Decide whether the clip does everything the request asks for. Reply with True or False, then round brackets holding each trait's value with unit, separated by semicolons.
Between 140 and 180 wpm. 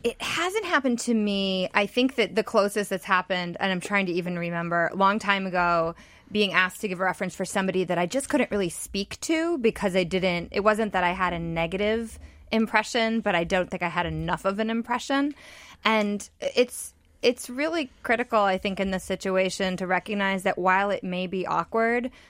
False (205 wpm)